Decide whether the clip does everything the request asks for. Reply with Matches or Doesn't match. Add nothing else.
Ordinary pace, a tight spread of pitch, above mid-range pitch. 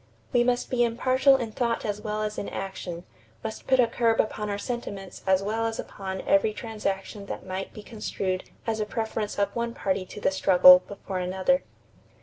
Doesn't match